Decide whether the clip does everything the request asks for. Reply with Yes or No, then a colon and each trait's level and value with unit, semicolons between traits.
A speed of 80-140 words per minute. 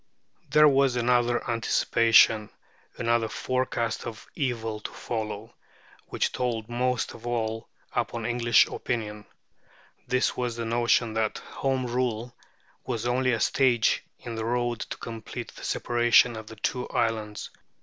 Yes: slow, 135 wpm